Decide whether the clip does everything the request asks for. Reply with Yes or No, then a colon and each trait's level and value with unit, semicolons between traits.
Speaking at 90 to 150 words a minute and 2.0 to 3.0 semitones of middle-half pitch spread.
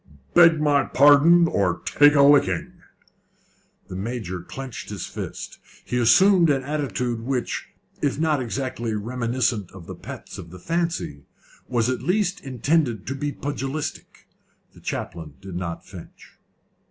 No: average, 140 wpm; average, 5.2 semitones